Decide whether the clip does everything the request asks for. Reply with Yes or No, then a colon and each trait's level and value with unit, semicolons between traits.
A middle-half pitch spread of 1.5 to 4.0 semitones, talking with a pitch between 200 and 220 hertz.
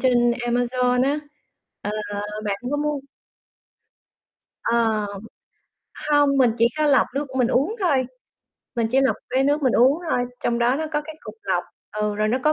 No: average, 3.4 semitones; very high, 255 Hz